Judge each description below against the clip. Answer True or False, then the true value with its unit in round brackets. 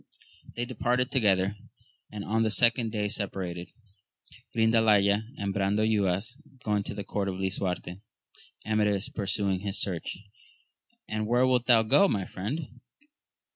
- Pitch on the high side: False (105 Hz)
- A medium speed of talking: False (130 wpm)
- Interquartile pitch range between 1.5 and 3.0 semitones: True (2.6 semitones)